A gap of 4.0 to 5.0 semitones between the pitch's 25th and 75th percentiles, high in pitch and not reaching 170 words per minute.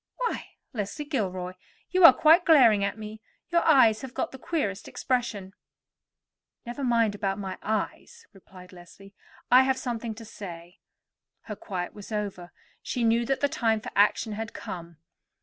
Yes: average, 4.7 semitones; high, 220 Hz; average, 160 wpm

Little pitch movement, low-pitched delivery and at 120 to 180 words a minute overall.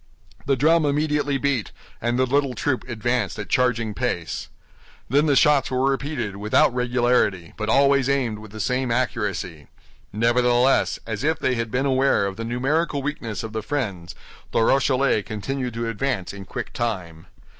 No: average, 4.1 semitones; low, 125 Hz; average, 165 wpm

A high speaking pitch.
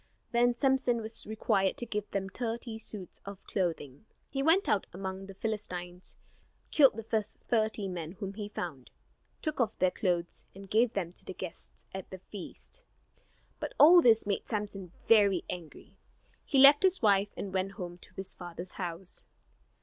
Yes: high, 200 Hz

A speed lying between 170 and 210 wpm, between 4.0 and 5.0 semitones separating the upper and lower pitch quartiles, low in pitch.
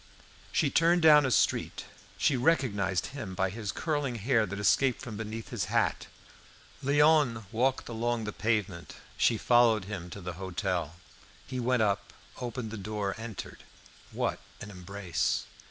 No: average, 150 wpm; average, 4.4 semitones; low, 110 Hz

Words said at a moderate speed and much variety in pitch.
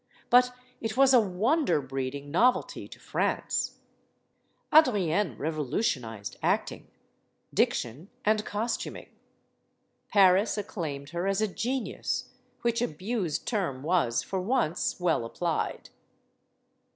No: slow, 105 wpm; wide, 7.2 semitones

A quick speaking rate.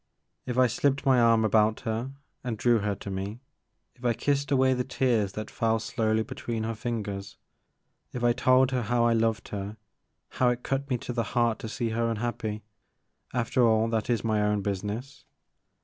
Yes: fast, 210 wpm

